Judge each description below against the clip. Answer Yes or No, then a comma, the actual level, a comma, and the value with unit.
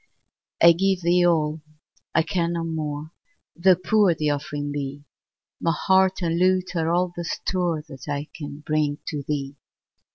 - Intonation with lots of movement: No, average, 3.2 semitones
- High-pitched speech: No, medium, 165 Hz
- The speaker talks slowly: No, average, 160 wpm